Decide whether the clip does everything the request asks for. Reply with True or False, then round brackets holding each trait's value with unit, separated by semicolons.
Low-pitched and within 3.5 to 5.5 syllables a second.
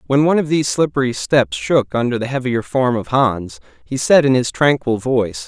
True (125 Hz; 5.3 syllables/s)